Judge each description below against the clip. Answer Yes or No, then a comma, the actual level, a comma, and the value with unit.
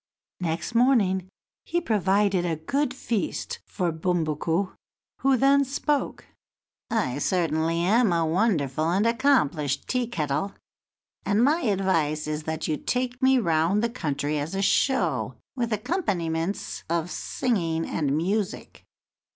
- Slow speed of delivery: Yes, slow, 125 wpm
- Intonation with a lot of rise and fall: Yes, wide, 6.7 semitones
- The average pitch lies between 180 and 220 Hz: Yes, medium, 185 Hz